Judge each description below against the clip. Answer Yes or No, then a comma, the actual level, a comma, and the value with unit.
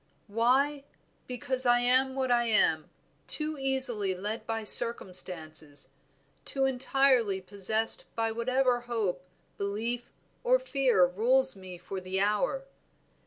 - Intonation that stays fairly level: No, average, 5.0 semitones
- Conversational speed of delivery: No, slow, 120 wpm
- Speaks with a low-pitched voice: No, high, 235 Hz